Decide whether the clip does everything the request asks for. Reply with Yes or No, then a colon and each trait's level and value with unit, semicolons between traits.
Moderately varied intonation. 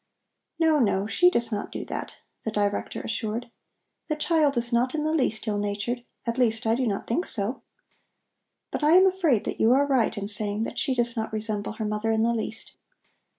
Yes: average, 3.8 semitones